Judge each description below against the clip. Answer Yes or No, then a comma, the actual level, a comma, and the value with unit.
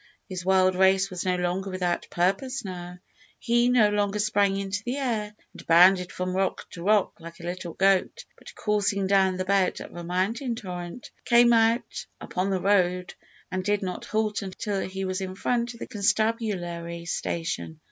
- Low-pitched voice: No, high, 190 Hz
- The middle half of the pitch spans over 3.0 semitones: No, narrow, 2.5 semitones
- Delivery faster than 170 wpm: Yes, average, 180 wpm